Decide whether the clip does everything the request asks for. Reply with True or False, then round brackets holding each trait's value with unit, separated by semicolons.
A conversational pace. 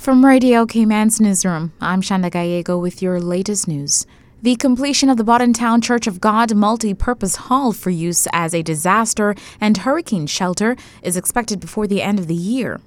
True (180 wpm)